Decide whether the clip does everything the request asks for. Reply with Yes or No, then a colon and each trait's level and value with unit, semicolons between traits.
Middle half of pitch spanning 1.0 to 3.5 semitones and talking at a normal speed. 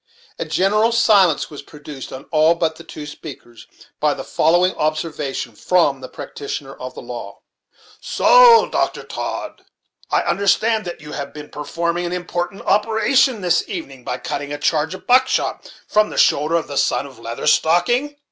No: average, 5.3 semitones; average, 170 wpm